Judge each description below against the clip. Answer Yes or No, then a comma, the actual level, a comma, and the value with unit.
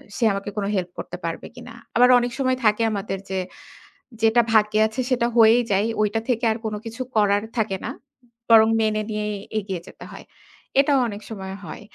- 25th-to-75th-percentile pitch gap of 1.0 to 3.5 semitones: Yes, average, 2.8 semitones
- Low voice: No, high, 220 Hz